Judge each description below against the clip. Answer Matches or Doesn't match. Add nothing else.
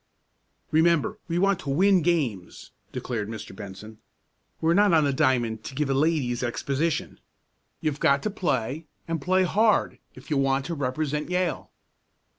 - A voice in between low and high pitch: Matches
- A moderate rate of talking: Matches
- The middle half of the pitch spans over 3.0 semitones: Matches